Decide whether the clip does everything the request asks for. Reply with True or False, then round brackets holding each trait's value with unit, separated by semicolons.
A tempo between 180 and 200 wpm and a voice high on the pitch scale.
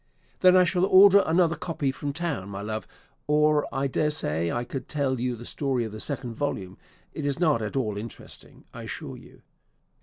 False (190 wpm; 140 Hz)